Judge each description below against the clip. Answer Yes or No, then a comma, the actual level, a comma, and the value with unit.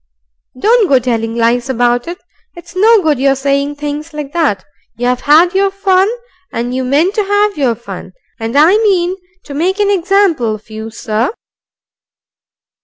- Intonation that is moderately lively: No, wide, 7.6 semitones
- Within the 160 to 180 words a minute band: Yes, average, 165 wpm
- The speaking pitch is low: No, very high, 295 Hz